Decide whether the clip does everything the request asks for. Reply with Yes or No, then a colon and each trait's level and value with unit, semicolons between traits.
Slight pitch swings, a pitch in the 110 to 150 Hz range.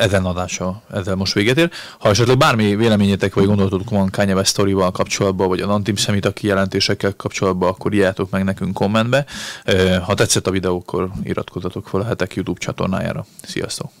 No: narrow, 1.7 semitones; low, 100 Hz